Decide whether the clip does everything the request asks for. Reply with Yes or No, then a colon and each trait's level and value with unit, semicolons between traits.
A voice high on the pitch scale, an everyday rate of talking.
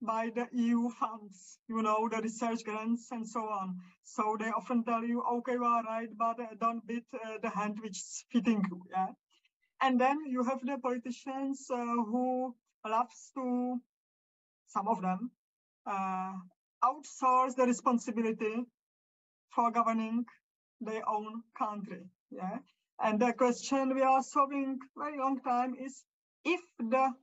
Yes: high, 235 Hz; average, 150 wpm